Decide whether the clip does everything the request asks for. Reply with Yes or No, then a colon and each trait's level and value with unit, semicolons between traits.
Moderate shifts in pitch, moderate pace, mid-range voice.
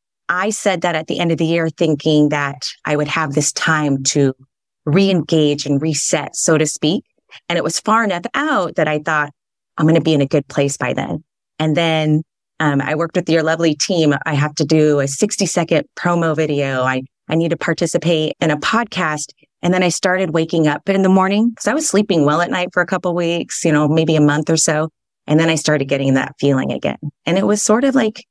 No: average, 3.0 semitones; fast, 235 wpm; medium, 160 Hz